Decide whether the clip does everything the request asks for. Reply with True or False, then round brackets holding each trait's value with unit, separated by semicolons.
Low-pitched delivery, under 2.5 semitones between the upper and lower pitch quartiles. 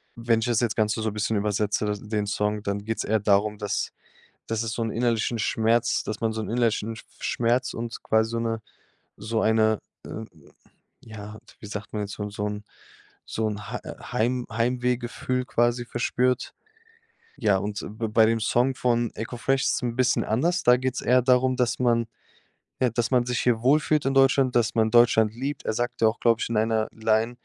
True (115 Hz; 2.1 semitones)